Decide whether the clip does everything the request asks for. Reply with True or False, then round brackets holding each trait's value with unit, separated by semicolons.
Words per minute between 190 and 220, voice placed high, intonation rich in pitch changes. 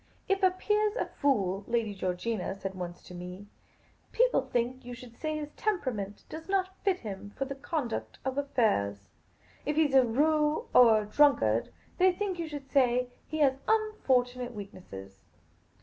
False (180 wpm; 255 Hz; 7.3 semitones)